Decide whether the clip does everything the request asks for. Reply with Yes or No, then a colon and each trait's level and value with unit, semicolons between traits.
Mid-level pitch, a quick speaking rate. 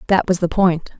Yes: medium, 180 Hz; fast, 240 wpm